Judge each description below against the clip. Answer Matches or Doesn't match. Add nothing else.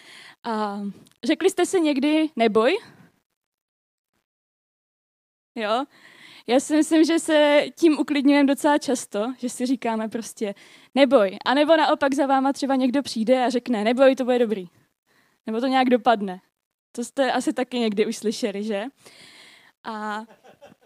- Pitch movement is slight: Doesn't match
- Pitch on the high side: Matches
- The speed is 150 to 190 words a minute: Doesn't match